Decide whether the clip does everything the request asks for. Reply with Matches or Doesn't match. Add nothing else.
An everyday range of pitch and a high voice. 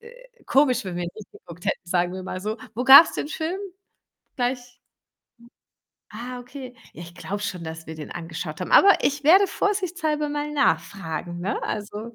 Doesn't match